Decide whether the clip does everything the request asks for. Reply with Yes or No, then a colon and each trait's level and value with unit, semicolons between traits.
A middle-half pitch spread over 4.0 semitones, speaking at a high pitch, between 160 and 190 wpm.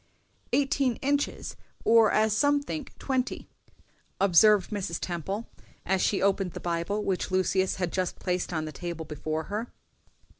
No: average, 4.4 semitones; high, 195 Hz; average, 145 wpm